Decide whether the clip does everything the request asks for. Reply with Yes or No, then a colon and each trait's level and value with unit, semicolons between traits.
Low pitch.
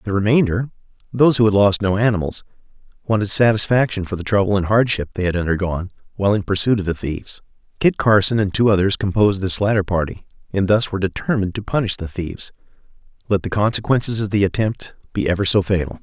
Yes: low, 100 Hz